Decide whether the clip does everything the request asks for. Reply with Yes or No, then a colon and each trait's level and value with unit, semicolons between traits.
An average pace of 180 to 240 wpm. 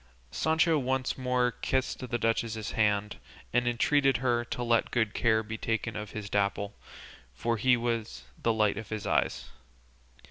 No: average, 155 wpm